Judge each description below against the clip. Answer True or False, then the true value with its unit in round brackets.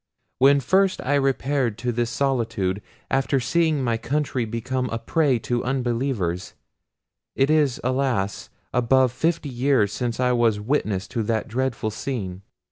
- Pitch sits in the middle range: False (125 Hz)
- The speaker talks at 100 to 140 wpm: True (135 wpm)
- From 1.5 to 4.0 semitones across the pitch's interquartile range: True (3.2 semitones)